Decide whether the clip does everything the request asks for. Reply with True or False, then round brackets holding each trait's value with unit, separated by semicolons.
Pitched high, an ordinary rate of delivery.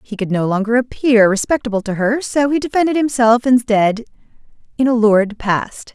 True (235 Hz; 170 wpm)